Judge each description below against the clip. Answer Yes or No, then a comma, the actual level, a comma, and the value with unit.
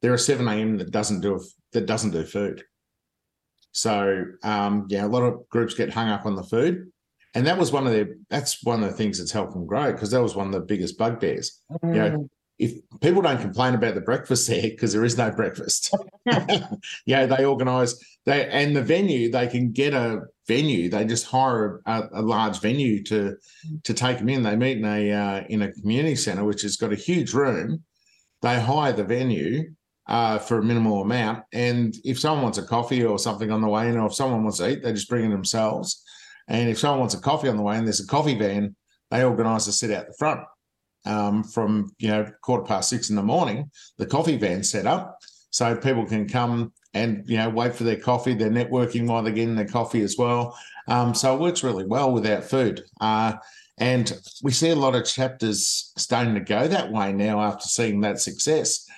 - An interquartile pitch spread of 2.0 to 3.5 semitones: Yes, average, 3.1 semitones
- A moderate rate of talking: No, fast, 220 wpm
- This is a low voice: Yes, low, 115 Hz